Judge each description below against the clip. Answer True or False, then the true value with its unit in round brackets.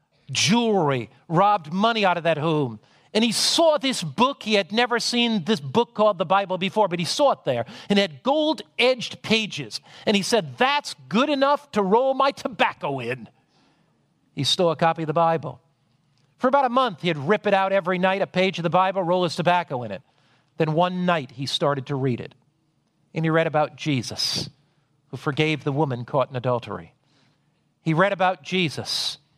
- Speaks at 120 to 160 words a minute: False (195 wpm)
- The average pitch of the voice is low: False (175 Hz)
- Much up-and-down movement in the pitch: True (6.3 semitones)